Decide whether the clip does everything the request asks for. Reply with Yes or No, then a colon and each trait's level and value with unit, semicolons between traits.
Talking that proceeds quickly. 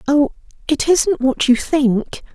No: average, 155 wpm